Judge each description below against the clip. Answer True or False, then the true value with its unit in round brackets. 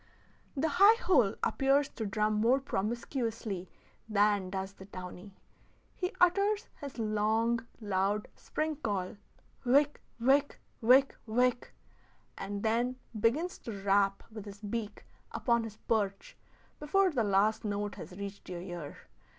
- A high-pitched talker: True (220 Hz)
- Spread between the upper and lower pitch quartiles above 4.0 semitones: True (4.9 semitones)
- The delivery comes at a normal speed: False (130 wpm)